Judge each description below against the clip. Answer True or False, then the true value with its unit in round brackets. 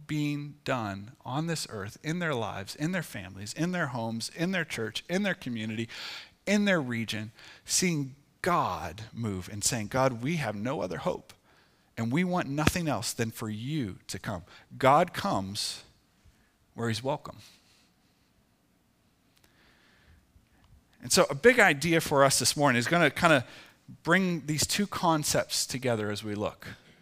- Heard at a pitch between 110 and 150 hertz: True (135 Hz)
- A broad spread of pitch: True (6.1 semitones)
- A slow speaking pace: False (160 wpm)